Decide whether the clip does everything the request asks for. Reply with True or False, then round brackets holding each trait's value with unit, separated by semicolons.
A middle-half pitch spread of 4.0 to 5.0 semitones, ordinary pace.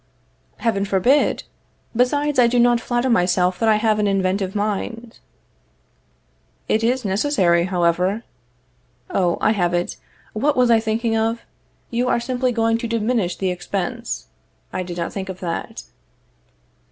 True (4.3 semitones; 145 wpm)